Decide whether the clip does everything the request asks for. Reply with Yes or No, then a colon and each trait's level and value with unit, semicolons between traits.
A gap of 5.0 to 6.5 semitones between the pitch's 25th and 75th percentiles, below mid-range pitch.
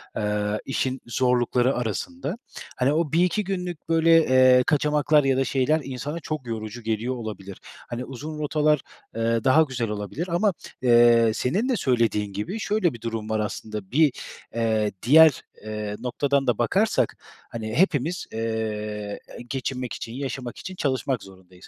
Yes: wide, 5.4 semitones; low, 125 Hz